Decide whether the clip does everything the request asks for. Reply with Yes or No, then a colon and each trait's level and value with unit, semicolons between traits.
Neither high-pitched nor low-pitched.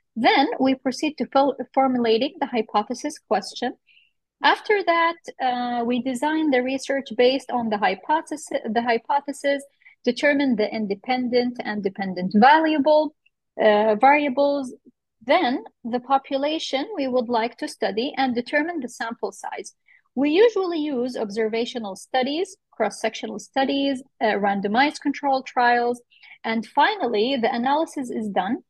No: very high, 260 Hz